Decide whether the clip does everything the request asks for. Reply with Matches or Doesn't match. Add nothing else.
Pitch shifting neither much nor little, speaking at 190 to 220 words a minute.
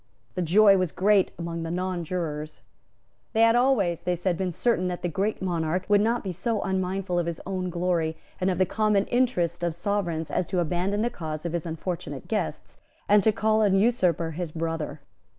Matches